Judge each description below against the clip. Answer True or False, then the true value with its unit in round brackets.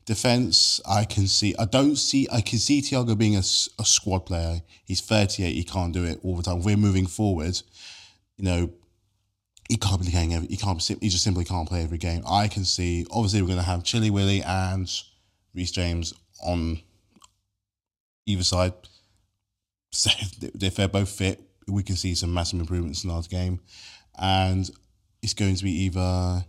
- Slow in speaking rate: False (180 wpm)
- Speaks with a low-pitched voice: True (95 Hz)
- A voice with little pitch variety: True (2.2 semitones)